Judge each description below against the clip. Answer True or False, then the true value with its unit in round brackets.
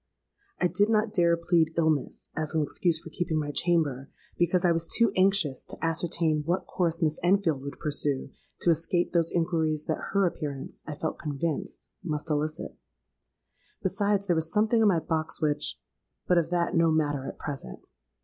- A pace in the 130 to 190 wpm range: True (170 wpm)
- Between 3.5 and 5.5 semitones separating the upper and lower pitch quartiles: False (2.6 semitones)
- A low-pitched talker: False (165 Hz)